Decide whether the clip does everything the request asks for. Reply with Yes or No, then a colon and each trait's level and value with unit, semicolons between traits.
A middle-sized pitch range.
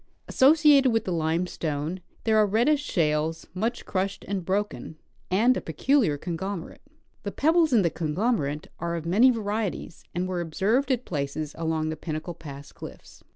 No: wide, 6.1 semitones